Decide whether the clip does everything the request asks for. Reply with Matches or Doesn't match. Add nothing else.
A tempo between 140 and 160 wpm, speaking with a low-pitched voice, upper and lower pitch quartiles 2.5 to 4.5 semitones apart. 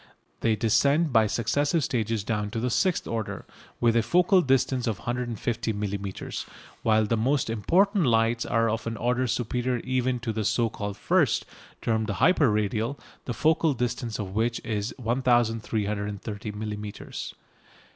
Matches